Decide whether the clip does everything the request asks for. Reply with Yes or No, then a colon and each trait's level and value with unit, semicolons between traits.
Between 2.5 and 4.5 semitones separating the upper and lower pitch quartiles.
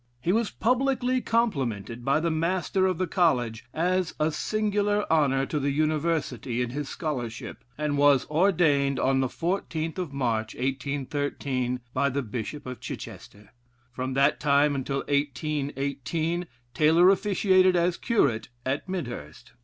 No: average, 5.0 semitones